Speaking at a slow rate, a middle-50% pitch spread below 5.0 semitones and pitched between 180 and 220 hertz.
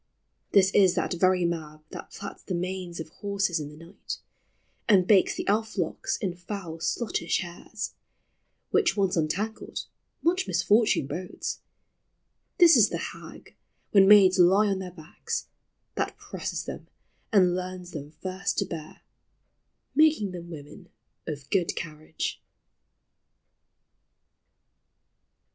Yes: slow, 130 wpm; average, 3.3 semitones; medium, 185 Hz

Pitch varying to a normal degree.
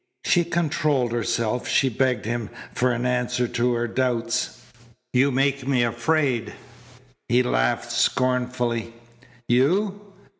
No: narrow, 2.2 semitones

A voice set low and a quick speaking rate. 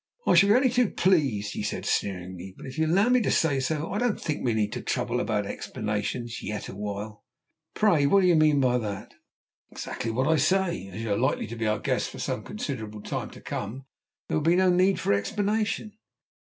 Yes: low, 130 Hz; fast, 215 wpm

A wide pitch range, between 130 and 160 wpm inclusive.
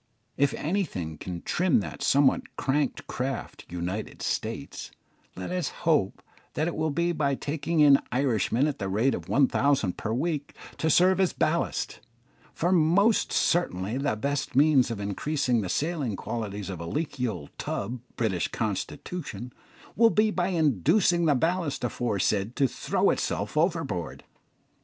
Yes: wide, 7.2 semitones; average, 150 wpm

